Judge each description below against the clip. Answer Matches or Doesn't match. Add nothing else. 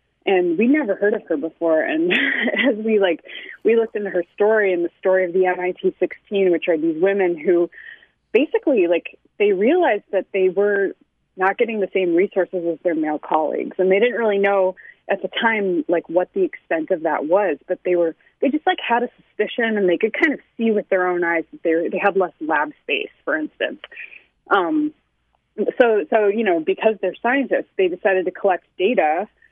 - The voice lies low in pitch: Doesn't match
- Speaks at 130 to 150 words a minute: Doesn't match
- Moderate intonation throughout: Doesn't match